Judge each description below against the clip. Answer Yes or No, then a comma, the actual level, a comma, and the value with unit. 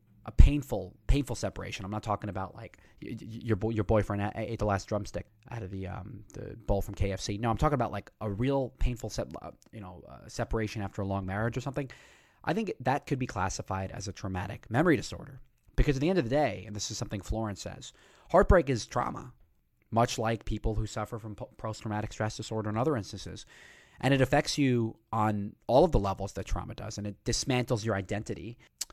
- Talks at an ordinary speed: No, fast, 210 wpm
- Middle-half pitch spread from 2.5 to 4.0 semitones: Yes, average, 2.9 semitones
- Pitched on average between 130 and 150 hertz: No, low, 110 Hz